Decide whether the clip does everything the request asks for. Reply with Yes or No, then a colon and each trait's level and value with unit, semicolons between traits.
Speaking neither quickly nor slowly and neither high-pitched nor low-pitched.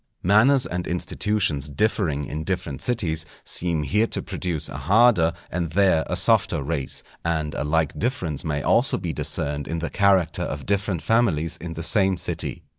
No: average, 175 wpm; very low, 85 Hz